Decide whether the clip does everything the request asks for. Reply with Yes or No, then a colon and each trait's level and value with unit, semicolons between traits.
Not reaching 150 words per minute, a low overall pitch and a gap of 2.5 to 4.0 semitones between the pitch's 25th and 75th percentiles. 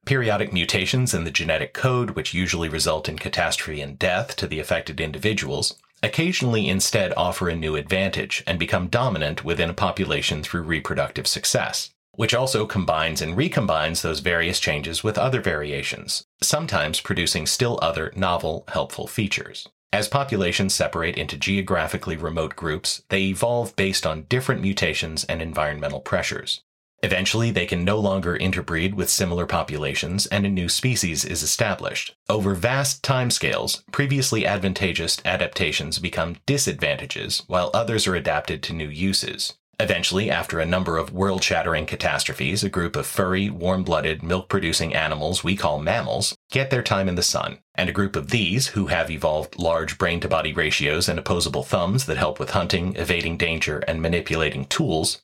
No: average, 155 wpm; very low, 90 Hz; average, 3.5 semitones